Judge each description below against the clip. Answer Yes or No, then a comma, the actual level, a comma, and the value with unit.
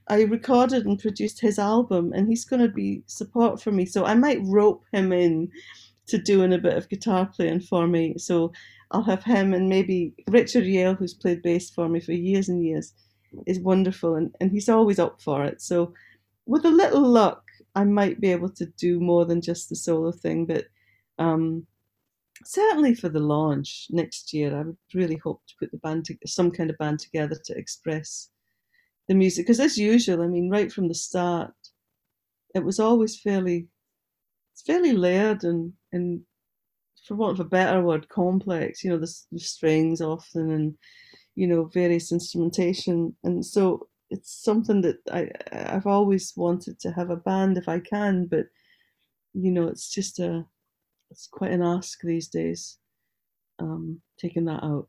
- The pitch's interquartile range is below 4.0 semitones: Yes, average, 3.3 semitones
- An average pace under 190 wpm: Yes, average, 180 wpm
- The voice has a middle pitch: Yes, medium, 175 Hz